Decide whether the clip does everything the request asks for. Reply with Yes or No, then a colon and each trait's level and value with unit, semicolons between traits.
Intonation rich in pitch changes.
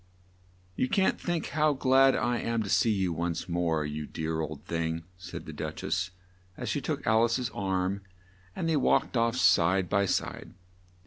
Yes: wide, 6.4 semitones